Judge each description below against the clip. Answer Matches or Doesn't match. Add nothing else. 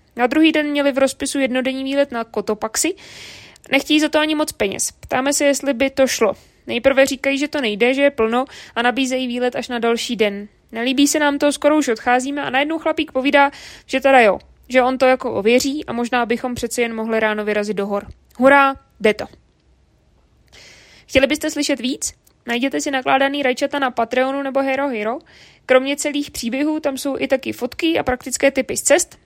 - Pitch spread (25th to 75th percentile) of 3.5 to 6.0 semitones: Doesn't match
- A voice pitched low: Doesn't match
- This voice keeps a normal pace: Doesn't match